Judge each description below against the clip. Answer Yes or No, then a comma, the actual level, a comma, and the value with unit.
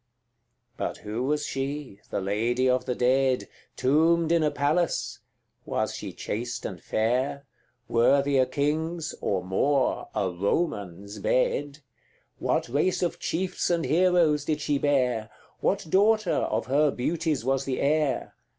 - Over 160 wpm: No, average, 140 wpm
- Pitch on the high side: No, medium, 140 Hz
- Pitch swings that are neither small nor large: Yes, average, 4.2 semitones